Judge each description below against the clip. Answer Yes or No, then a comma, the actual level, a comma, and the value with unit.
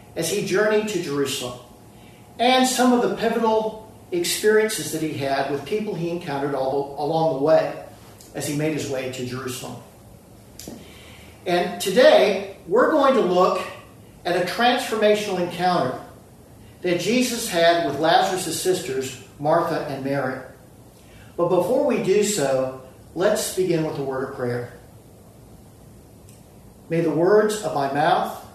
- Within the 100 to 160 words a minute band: Yes, average, 140 wpm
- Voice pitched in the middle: Yes, medium, 155 Hz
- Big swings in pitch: Yes, wide, 6.5 semitones